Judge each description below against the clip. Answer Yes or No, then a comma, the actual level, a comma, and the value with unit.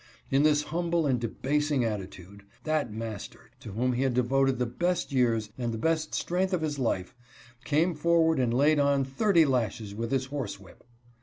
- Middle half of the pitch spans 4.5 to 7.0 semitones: Yes, average, 4.9 semitones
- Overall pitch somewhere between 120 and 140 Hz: Yes, low, 135 Hz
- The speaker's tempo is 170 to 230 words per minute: Yes, average, 180 wpm